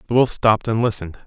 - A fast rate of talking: Yes, fast, 240 wpm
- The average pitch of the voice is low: Yes, low, 110 Hz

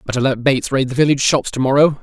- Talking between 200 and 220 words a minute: No, fast, 265 wpm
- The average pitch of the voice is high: No, low, 135 Hz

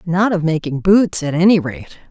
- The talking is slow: No, average, 200 wpm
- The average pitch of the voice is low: No, medium, 175 Hz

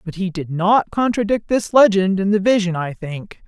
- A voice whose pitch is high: Yes, high, 195 Hz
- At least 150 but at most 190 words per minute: No, fast, 205 wpm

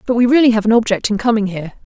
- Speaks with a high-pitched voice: Yes, high, 220 Hz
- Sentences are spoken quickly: Yes, fast, 280 wpm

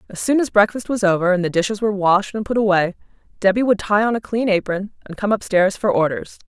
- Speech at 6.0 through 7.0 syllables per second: Yes, 6.2 syllables/s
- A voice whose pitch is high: Yes, high, 200 Hz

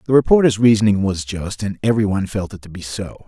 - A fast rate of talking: Yes, fast, 240 wpm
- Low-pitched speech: Yes, low, 105 Hz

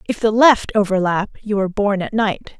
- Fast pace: Yes, fast, 210 wpm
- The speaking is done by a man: No, female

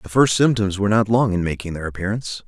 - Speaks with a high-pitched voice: No, low, 105 Hz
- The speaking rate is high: Yes, fast, 240 wpm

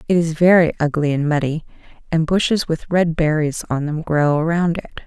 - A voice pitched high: No, medium, 160 Hz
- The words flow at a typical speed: Yes, average, 190 wpm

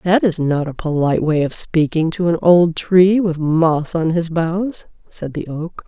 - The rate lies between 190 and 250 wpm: Yes, fast, 205 wpm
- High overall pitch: No, medium, 165 Hz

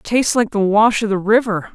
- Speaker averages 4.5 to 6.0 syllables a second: Yes, 5.3 syllables/s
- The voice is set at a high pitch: Yes, high, 215 Hz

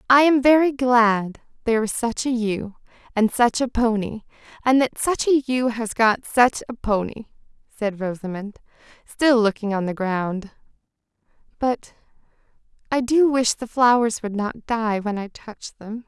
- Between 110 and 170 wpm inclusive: Yes, average, 160 wpm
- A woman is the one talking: Yes, female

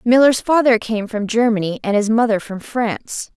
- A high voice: Yes, high, 225 Hz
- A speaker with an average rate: Yes, average, 175 wpm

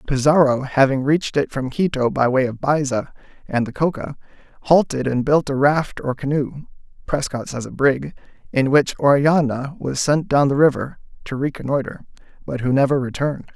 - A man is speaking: Yes, male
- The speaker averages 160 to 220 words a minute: Yes, average, 170 wpm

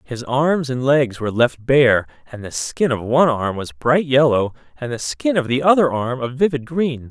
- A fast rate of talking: Yes, fast, 220 wpm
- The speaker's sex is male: Yes, male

